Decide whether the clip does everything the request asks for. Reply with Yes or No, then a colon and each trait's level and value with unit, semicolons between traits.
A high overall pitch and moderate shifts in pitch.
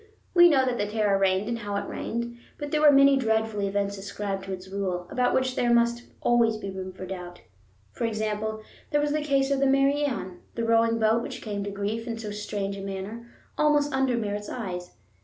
Yes: high, 220 Hz; average, 4.1 semitones